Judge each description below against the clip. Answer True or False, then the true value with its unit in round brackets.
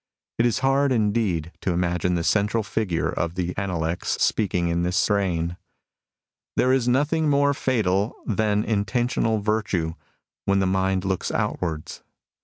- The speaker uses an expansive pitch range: False (4.6 semitones)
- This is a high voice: False (100 Hz)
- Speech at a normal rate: True (150 wpm)